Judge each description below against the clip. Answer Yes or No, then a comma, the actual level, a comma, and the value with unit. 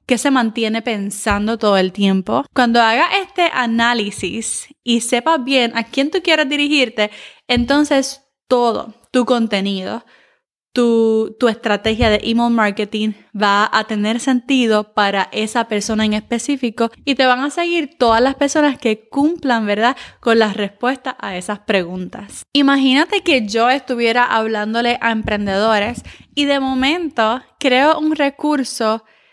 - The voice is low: No, high, 235 Hz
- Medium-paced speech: Yes, average, 140 wpm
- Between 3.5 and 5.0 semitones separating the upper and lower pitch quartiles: Yes, average, 4.1 semitones